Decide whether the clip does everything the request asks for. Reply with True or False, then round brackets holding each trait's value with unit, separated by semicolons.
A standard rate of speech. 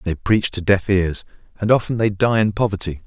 False (215 wpm)